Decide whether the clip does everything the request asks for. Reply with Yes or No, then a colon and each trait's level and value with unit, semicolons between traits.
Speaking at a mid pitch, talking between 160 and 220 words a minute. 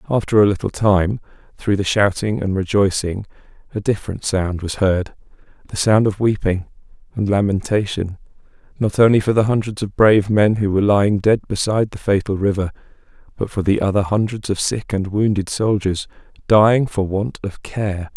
No: low, 100 Hz; average, 170 wpm